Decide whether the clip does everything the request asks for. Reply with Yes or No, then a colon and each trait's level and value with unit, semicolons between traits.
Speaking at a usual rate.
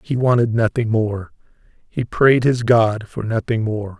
Yes: average, 165 wpm